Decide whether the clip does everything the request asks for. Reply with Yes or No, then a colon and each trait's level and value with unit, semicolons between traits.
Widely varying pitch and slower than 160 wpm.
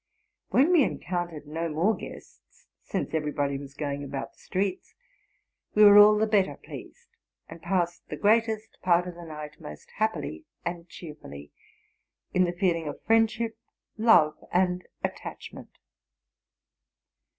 Yes: wide, 5.7 semitones; slow, 135 wpm